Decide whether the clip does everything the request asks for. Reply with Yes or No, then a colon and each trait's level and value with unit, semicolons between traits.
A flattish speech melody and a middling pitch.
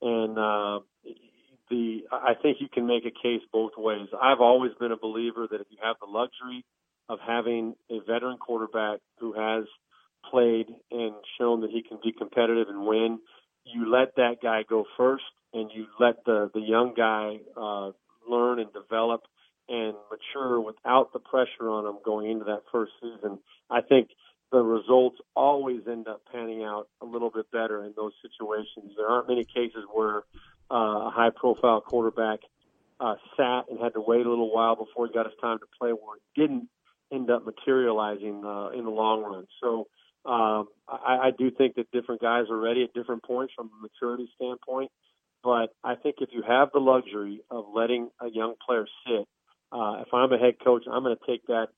No: narrow, 2.0 semitones; low, 115 Hz